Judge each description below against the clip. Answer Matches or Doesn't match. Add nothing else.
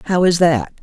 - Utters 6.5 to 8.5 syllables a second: Doesn't match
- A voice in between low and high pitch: Matches